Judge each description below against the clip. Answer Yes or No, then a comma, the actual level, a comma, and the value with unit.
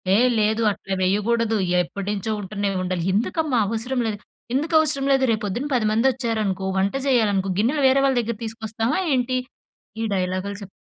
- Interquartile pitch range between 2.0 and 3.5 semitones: No, average, 4.2 semitones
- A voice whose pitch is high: Yes, high, 220 Hz